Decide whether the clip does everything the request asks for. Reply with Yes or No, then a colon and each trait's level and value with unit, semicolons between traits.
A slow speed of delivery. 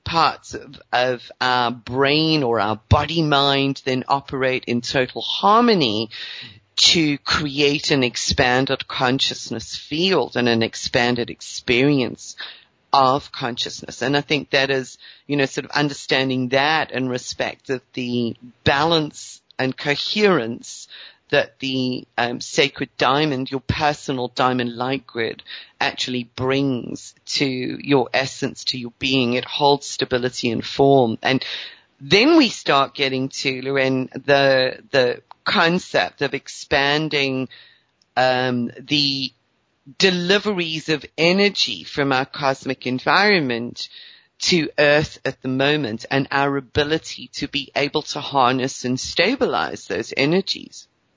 Yes: slow, 125 wpm